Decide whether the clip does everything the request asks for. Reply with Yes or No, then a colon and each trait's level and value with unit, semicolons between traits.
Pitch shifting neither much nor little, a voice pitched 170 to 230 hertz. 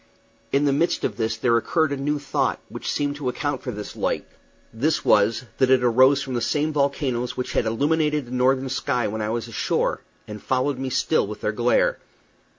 No: average, 3.4 semitones; low, 130 Hz